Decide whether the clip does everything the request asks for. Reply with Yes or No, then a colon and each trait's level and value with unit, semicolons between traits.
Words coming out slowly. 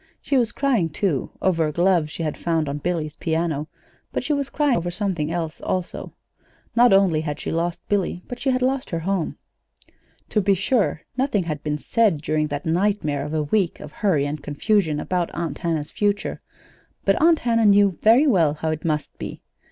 No: average, 195 wpm